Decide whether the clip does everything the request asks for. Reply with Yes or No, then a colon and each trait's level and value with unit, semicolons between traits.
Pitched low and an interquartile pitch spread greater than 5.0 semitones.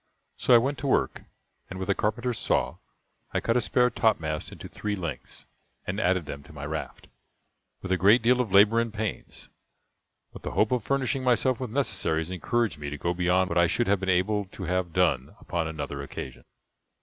Yes: very low, 95 Hz; wide, 5.6 semitones